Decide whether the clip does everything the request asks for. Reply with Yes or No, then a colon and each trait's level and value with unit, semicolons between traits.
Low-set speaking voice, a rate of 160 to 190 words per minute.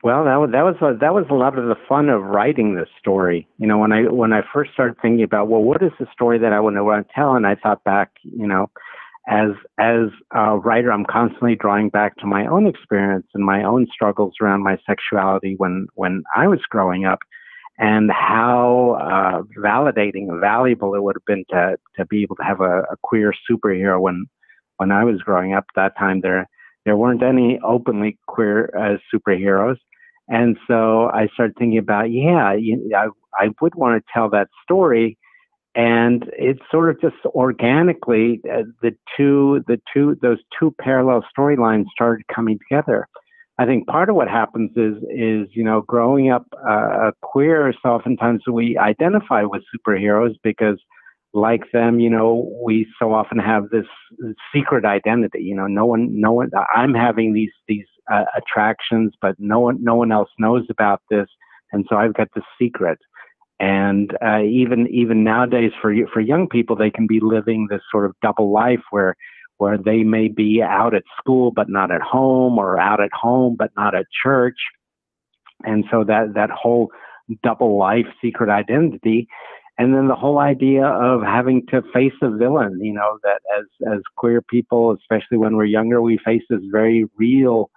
Yes: low, 115 Hz; average, 185 wpm